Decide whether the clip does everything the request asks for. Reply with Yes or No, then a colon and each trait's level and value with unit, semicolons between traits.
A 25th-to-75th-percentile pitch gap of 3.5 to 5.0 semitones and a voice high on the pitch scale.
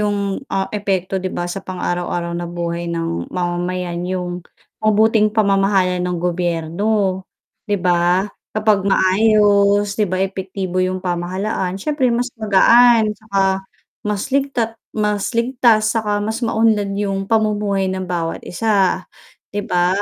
No: average, 3.0 semitones; high, 195 Hz